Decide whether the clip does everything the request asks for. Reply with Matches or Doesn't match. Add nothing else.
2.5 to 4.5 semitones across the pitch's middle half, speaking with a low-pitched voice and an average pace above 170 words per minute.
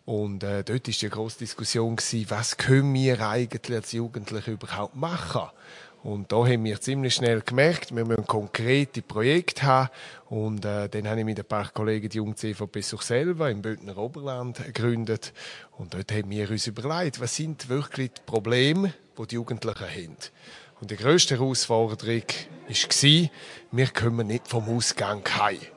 Doesn't match